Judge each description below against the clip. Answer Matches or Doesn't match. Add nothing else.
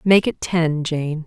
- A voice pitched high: Doesn't match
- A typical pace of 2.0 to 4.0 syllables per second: Matches